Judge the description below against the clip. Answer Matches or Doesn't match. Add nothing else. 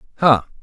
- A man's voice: Matches